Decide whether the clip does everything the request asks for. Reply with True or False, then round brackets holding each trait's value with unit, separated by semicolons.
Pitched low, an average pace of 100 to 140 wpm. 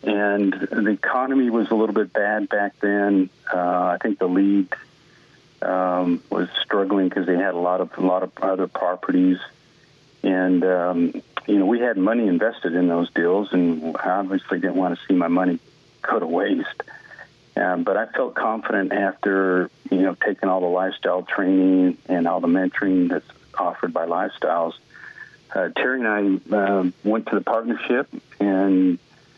False (95 Hz; 170 wpm)